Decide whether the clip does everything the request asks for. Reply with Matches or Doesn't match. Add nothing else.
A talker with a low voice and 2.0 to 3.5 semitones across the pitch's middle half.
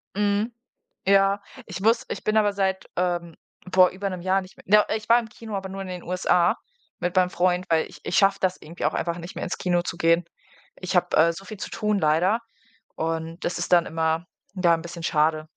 Doesn't match